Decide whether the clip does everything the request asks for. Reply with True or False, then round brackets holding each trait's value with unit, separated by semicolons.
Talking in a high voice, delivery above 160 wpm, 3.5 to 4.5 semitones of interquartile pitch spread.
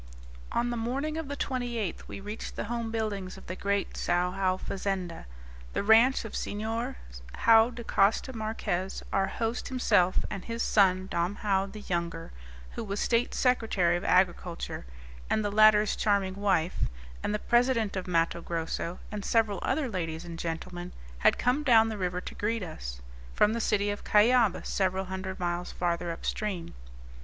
True (200 Hz; 170 wpm; 3.8 semitones)